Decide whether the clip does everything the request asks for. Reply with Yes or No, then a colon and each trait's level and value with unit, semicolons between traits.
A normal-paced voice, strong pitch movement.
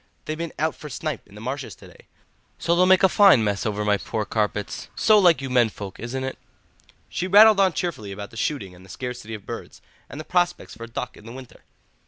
No: fast, 235 wpm; wide, 8.1 semitones